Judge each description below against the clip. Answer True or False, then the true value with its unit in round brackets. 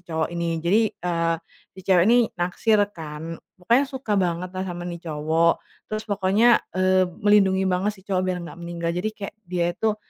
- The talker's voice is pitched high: False (180 Hz)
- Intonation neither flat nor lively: True (3.1 semitones)